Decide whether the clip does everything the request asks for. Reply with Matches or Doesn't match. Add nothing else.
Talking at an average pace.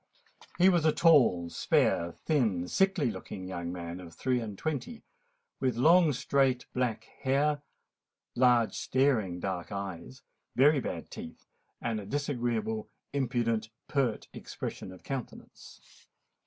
Doesn't match